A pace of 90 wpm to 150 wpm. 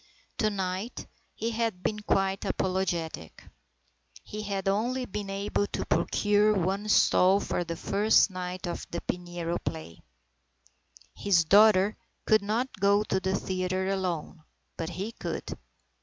Yes: slow, 135 wpm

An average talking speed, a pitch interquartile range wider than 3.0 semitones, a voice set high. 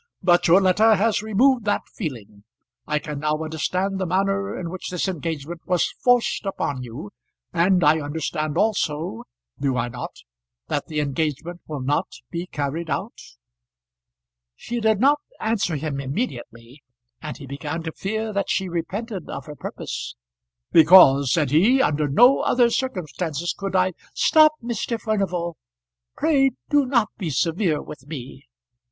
No: average, 150 wpm; wide, 5.6 semitones; medium, 170 Hz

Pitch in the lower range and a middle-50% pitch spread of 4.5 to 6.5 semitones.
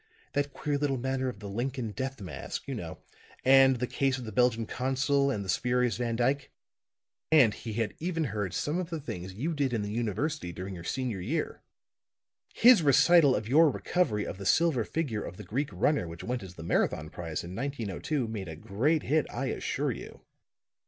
Yes: low, 125 Hz; wide, 5.5 semitones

